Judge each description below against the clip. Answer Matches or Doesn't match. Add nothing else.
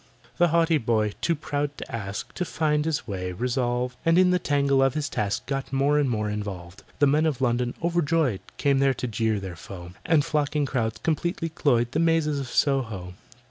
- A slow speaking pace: Doesn't match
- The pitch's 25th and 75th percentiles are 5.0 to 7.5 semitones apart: Matches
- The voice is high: Doesn't match